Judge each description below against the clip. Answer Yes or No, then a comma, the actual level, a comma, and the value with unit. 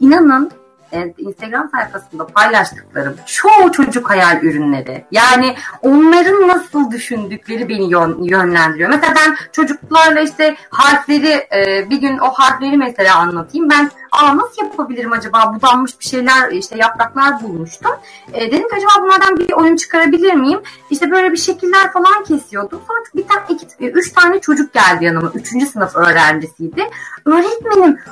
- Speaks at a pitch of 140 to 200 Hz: No, very high, 280 Hz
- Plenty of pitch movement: Yes, wide, 7.9 semitones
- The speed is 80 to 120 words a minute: No, average, 135 wpm